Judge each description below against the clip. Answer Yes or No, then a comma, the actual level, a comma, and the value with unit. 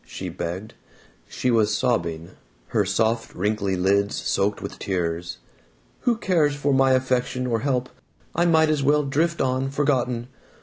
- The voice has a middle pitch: No, low, 125 Hz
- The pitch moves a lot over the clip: Yes, wide, 6.0 semitones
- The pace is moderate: Yes, average, 145 wpm